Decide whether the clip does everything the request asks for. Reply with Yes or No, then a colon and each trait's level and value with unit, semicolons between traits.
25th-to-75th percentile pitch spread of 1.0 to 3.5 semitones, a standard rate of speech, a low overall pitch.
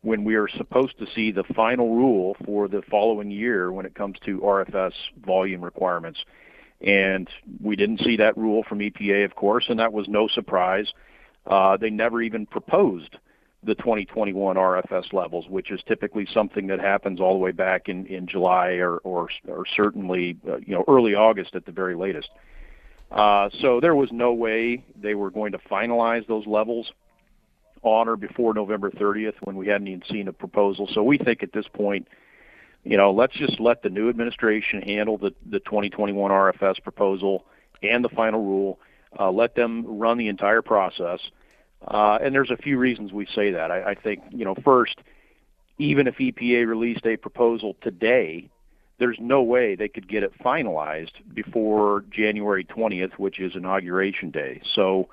Yes: average, 2.8 semitones; average, 180 wpm; low, 105 Hz